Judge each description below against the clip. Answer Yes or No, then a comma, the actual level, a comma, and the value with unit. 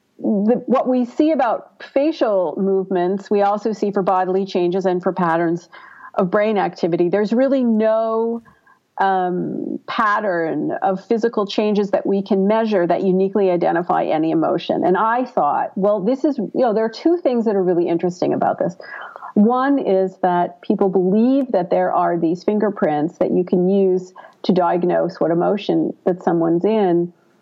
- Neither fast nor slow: Yes, average, 165 wpm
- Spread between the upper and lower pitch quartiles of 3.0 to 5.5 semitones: Yes, average, 3.8 semitones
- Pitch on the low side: No, high, 200 Hz